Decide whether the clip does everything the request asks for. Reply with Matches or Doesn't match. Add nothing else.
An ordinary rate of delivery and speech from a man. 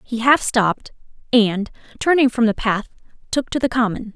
Doesn't match